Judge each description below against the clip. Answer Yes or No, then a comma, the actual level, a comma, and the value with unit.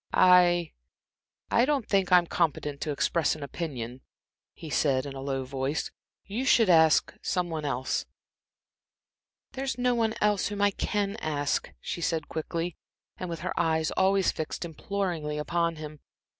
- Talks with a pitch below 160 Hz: No, medium, 170 Hz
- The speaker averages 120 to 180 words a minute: Yes, average, 155 wpm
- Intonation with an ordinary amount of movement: Yes, average, 4.7 semitones